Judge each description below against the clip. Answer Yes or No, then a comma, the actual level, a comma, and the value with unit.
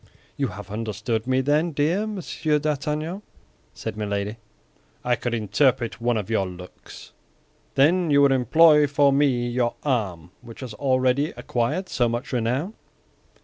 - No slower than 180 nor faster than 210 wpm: No, average, 145 wpm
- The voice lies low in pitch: Yes, low, 125 Hz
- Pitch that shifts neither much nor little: Yes, average, 4.6 semitones